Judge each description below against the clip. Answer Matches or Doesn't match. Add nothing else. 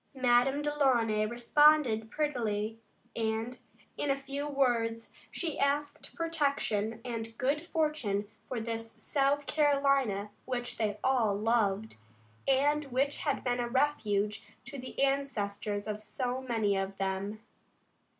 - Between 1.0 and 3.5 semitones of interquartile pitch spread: Doesn't match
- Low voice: Doesn't match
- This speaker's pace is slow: Matches